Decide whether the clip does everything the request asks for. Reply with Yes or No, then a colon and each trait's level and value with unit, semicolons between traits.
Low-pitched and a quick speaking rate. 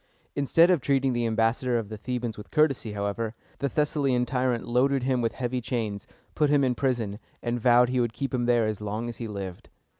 Yes: low, 120 Hz; fast, 210 wpm